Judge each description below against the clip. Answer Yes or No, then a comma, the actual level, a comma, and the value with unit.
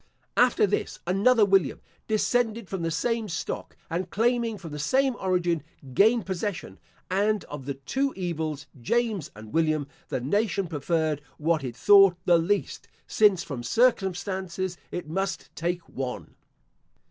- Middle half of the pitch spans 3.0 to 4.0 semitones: No, average, 4.8 semitones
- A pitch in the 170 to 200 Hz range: Yes, medium, 185 Hz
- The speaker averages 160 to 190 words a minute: No, average, 140 wpm